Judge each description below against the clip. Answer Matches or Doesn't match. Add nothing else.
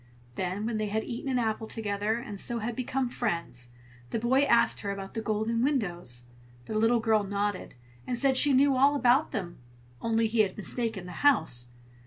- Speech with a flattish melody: Doesn't match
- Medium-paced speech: Matches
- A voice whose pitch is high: Matches